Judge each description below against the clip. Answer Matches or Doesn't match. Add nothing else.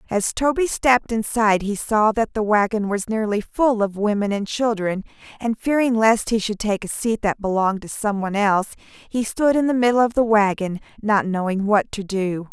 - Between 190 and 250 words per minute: Matches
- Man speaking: Doesn't match